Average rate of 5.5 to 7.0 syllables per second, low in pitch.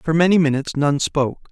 No: 6.1 syllables/s; medium, 150 Hz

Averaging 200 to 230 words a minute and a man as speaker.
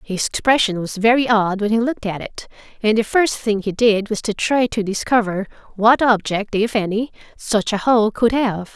No: fast, 205 wpm; female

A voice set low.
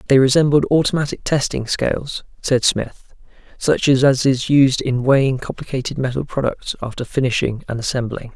Yes: low, 130 Hz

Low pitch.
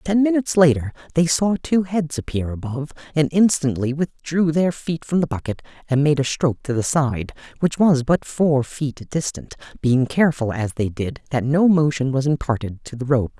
No: medium, 145 Hz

